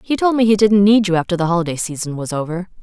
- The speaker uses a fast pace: Yes, fast, 275 wpm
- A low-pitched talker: No, high, 190 Hz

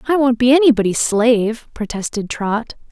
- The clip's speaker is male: No, female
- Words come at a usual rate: Yes, average, 145 wpm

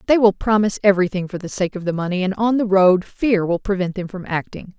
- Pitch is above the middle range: Yes, high, 195 Hz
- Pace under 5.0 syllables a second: No, 6.1 syllables/s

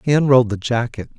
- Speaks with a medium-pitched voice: No, low, 125 Hz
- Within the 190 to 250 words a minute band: Yes, fast, 205 wpm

